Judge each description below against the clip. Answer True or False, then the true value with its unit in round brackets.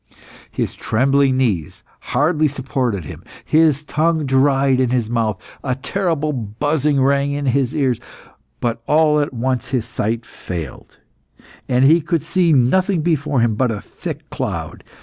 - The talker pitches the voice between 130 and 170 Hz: True (135 Hz)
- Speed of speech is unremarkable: True (150 wpm)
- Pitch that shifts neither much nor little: True (3.8 semitones)